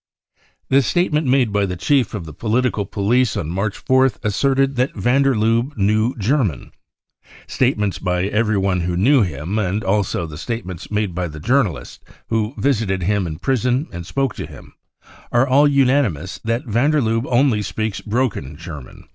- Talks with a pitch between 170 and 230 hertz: No, low, 110 Hz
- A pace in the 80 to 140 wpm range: No, average, 170 wpm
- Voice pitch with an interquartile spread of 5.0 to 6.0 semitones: Yes, wide, 5.4 semitones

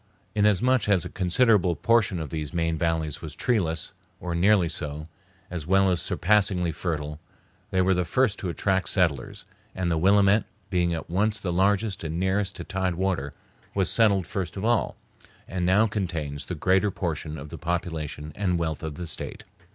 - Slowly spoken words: No, average, 175 wpm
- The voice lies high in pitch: No, very low, 90 Hz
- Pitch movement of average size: Yes, average, 3.2 semitones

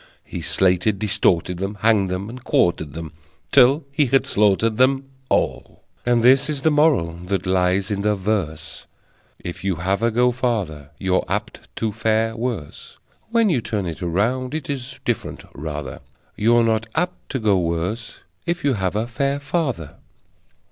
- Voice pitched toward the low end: Yes, low, 110 Hz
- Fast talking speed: No, average, 165 wpm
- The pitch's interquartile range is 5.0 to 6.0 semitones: Yes, wide, 5.6 semitones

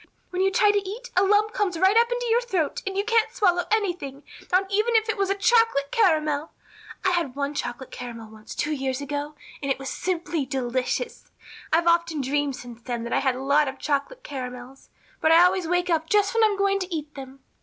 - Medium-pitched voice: No, very high, 330 Hz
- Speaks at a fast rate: Yes, fast, 220 wpm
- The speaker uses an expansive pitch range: Yes, wide, 6.4 semitones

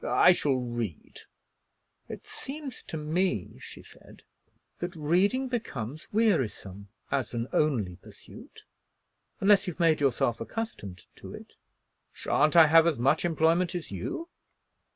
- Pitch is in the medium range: Yes, medium, 155 Hz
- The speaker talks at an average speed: No, slow, 130 wpm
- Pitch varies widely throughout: Yes, wide, 7.1 semitones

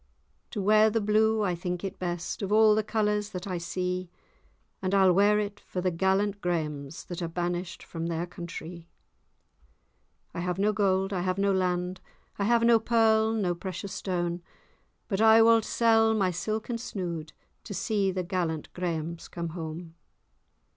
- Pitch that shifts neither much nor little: Yes, average, 3.3 semitones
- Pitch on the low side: No, high, 190 Hz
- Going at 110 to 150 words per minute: No, average, 170 wpm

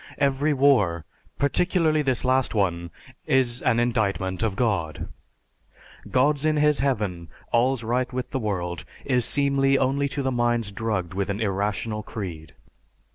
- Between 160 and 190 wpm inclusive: No, slow, 135 wpm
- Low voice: Yes, low, 120 Hz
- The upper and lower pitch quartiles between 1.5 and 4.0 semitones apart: No, wide, 5.5 semitones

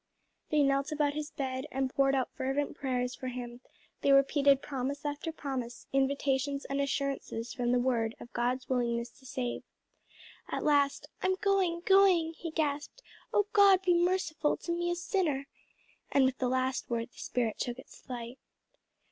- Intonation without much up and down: No, average, 3.3 semitones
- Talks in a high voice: Yes, very high, 275 Hz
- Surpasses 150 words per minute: Yes, average, 165 wpm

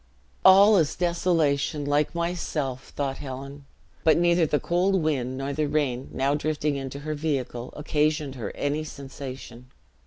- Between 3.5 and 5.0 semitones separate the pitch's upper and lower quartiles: No, average, 2.7 semitones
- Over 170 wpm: No, average, 145 wpm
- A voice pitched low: No, medium, 145 Hz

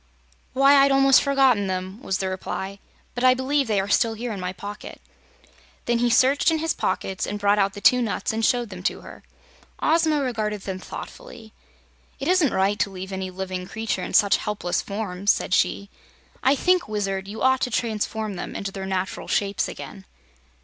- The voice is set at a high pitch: Yes, high, 210 Hz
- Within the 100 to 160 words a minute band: No, average, 190 wpm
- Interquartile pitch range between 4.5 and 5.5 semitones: Yes, average, 5.0 semitones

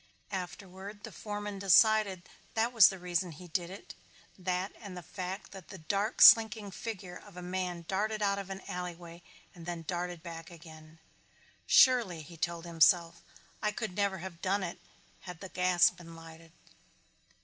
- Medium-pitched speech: Yes, medium, 180 Hz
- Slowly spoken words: No, average, 165 wpm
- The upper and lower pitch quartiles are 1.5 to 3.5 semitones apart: Yes, narrow, 2.6 semitones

